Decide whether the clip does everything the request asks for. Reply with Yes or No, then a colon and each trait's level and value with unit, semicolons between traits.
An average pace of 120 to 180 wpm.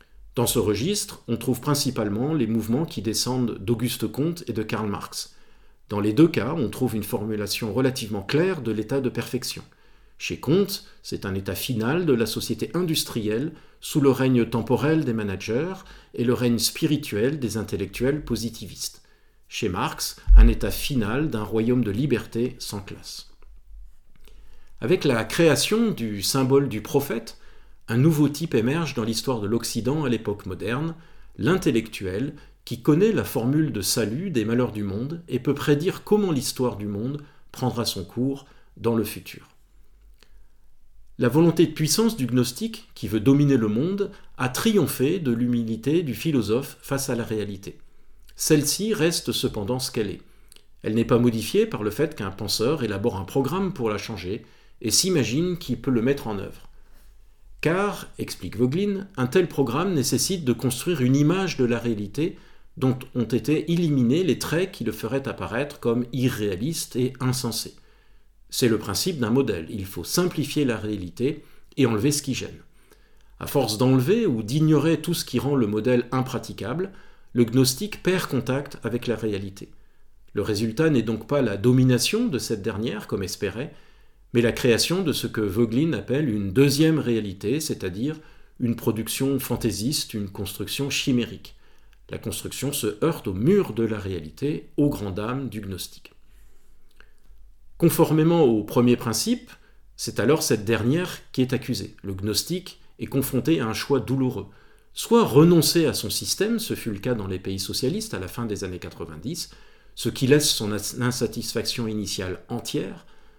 Yes: average, 160 wpm